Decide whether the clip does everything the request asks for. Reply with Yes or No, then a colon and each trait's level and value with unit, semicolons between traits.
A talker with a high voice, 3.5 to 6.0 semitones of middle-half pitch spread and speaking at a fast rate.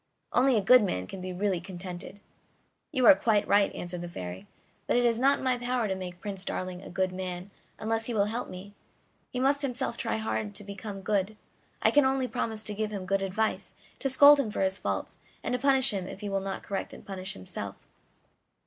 Yes: high, 205 Hz; average, 4.4 semitones; fast, 220 wpm